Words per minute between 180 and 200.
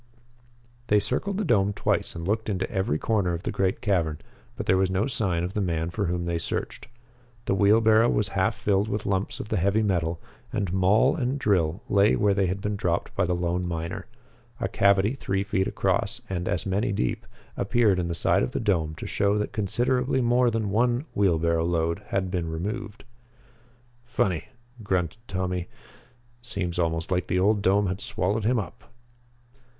Yes: average, 185 wpm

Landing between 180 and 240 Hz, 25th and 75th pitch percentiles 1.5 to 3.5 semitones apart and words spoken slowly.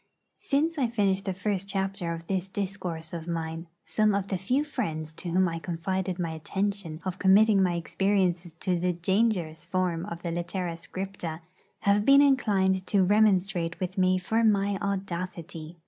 No: medium, 185 Hz; average, 2.8 semitones; average, 165 wpm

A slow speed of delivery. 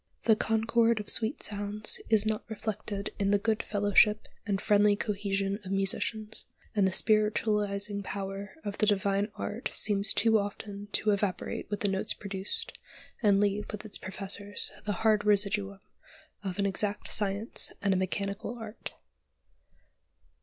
No: average, 145 wpm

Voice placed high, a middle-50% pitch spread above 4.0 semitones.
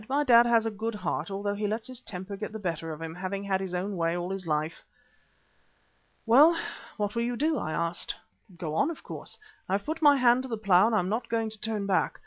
Yes: high, 205 Hz; average, 4.4 semitones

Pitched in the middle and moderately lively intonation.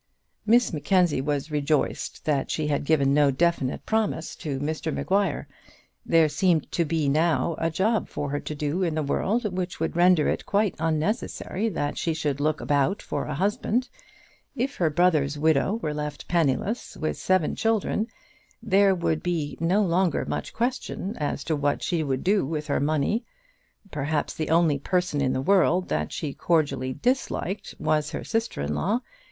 Yes: medium, 160 Hz; average, 4.4 semitones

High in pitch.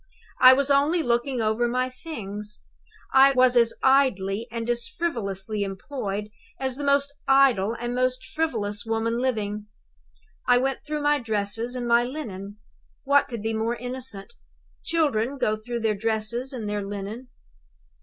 Yes: high, 240 Hz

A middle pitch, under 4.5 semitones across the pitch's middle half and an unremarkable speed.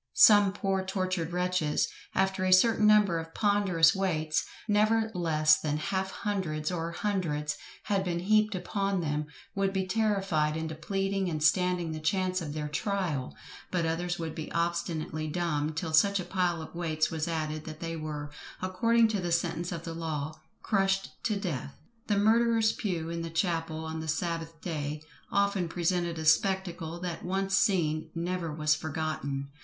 Yes: medium, 170 Hz; average, 3.5 semitones; average, 165 wpm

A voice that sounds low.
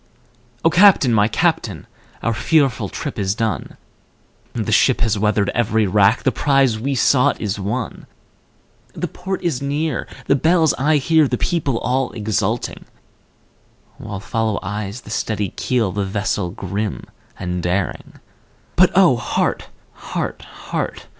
Yes: low, 115 Hz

